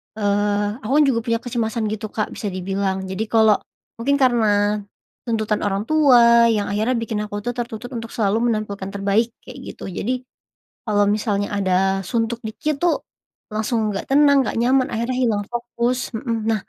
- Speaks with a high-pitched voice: Yes, high, 220 Hz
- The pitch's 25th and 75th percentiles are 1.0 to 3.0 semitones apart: Yes, average, 2.7 semitones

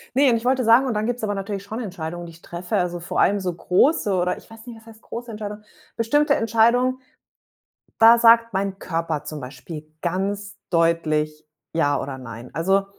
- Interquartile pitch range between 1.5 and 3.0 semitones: No, wide, 5.4 semitones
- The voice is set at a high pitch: Yes, high, 200 Hz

